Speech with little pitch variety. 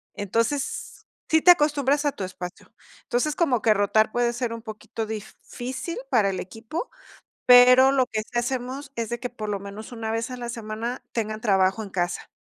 No: average, 3.2 semitones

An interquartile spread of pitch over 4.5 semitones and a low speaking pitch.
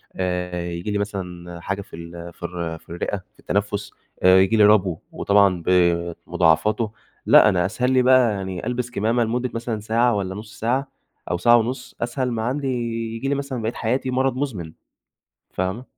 Yes: average, 4.9 semitones; low, 105 Hz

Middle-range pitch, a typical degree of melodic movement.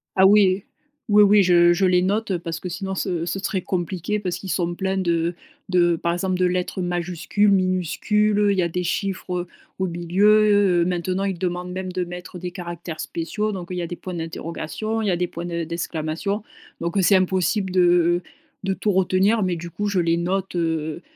No: medium, 180 Hz; narrow, 1.9 semitones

